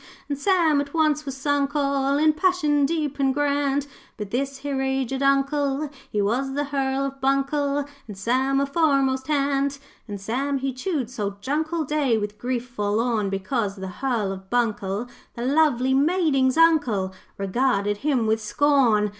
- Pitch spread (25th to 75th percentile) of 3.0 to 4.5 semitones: Yes, average, 3.6 semitones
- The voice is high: Yes, very high, 270 Hz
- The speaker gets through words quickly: No, average, 165 wpm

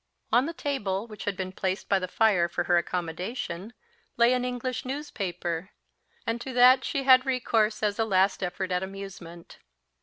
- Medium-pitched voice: No, high, 205 Hz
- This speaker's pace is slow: No, average, 175 wpm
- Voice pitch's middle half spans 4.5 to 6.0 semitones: Yes, average, 5.2 semitones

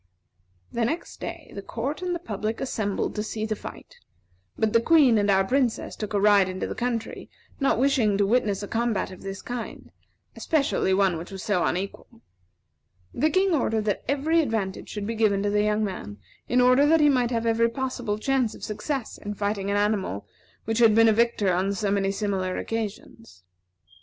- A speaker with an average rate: Yes, average, 195 wpm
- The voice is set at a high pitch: Yes, high, 220 Hz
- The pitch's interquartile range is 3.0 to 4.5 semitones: Yes, average, 3.7 semitones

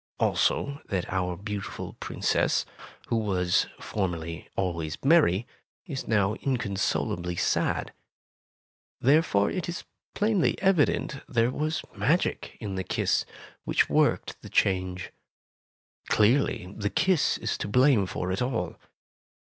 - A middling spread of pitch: No, wide, 7.3 semitones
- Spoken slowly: Yes, slow, 115 wpm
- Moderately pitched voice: No, low, 105 Hz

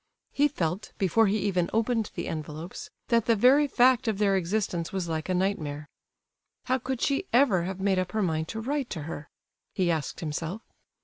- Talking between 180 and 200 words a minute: Yes, average, 190 wpm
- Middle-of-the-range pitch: No, high, 195 Hz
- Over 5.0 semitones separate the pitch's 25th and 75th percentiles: Yes, wide, 5.5 semitones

